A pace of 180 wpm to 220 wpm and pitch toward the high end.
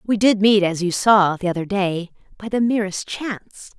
Yes: fast, 205 wpm; high, 200 Hz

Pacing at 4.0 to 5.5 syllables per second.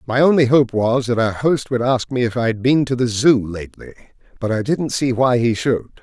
Yes: 5.3 syllables/s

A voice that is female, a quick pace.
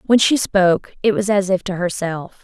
Yes: female; fast, 220 wpm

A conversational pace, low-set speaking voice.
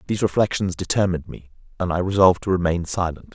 Yes: average, 180 wpm; very low, 90 Hz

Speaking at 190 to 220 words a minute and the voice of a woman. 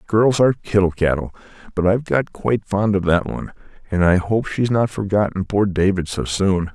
No: average, 195 wpm; male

